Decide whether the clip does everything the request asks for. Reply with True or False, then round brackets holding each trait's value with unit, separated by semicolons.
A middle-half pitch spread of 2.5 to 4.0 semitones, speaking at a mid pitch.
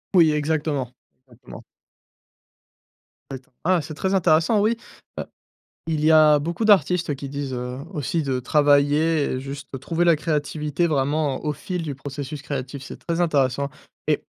True (2.8 semitones; 150 Hz)